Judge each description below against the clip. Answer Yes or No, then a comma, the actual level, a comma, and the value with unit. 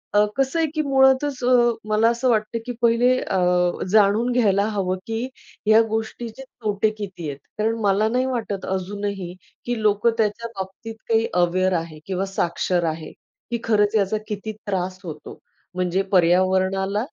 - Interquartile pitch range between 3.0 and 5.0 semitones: Yes, average, 3.5 semitones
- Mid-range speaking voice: No, high, 210 Hz